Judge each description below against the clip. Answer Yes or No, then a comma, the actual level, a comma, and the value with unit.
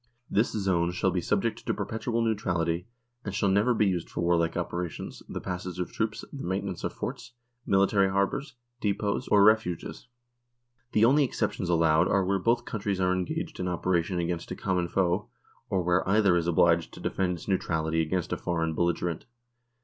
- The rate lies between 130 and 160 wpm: No, average, 175 wpm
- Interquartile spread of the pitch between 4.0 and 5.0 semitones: No, average, 2.9 semitones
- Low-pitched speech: Yes, very low, 95 Hz